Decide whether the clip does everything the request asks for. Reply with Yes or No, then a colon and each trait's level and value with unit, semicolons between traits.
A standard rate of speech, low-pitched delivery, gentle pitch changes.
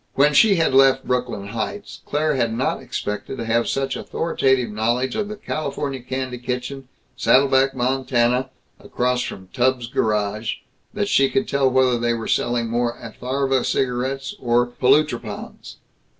Yes: average, 150 wpm; low, 130 Hz; narrow, 2.3 semitones